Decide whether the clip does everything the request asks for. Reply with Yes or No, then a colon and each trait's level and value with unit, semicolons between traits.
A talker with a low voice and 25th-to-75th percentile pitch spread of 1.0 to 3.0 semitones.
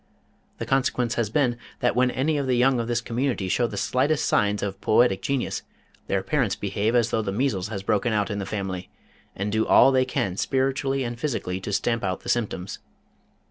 No: low, 115 Hz; average, 4.2 semitones